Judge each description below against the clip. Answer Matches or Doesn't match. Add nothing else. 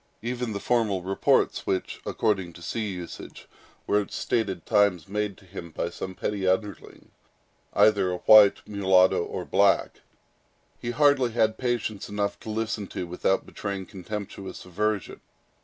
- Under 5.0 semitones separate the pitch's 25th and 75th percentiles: Matches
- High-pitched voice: Doesn't match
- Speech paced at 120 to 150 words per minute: Matches